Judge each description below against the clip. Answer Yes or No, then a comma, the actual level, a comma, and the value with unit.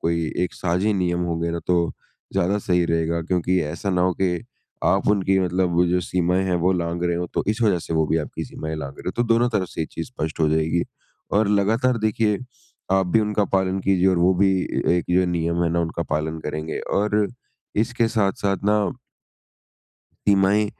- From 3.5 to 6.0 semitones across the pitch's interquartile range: No, average, 3.1 semitones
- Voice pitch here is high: No, very low, 90 Hz